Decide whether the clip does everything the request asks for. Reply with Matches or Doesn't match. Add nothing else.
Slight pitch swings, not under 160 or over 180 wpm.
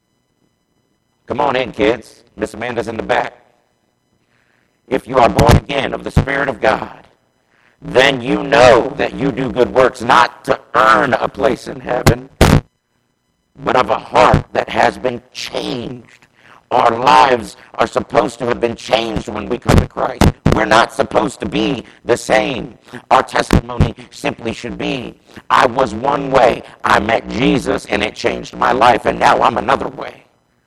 Matches